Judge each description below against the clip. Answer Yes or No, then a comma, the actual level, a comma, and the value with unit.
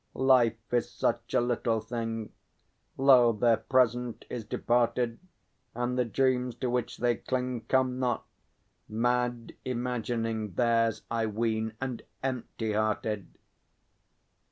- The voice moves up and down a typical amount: No, narrow, 1.7 semitones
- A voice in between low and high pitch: No, low, 120 Hz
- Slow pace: Yes, slow, 115 wpm